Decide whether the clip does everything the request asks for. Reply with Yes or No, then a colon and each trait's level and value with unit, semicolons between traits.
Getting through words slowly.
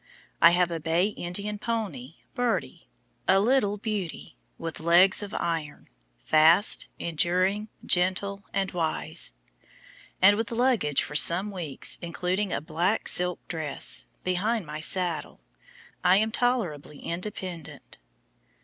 Yes: slow, 120 wpm